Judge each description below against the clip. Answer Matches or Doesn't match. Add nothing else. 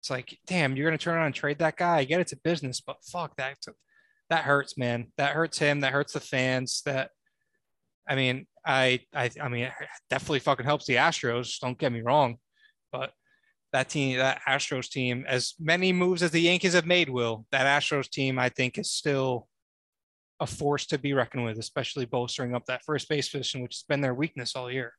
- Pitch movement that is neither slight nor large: Matches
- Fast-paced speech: Matches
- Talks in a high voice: Doesn't match